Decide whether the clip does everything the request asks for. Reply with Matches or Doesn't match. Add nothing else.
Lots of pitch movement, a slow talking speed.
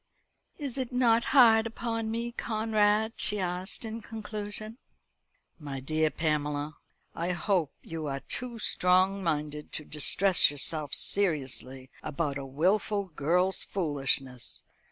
Matches